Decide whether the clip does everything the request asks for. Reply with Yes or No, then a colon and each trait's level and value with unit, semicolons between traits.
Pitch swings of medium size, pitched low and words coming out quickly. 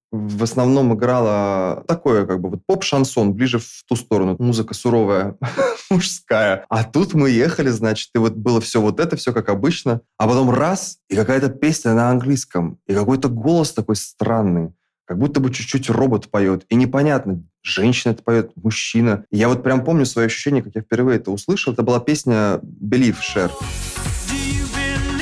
Yes: average, 3.9 semitones; low, 120 Hz; fast, 170 wpm